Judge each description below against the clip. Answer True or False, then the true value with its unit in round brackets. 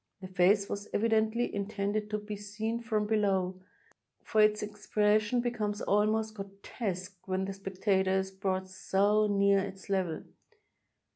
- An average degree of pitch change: False (1.9 semitones)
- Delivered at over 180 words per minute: False (140 wpm)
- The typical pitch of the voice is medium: False (205 Hz)